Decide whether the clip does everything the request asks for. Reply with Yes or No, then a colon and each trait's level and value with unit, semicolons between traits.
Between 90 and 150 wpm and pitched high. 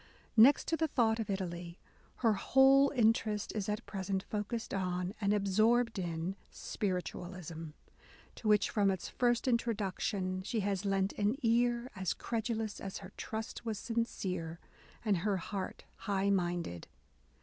Yes: average, 140 wpm; high, 205 Hz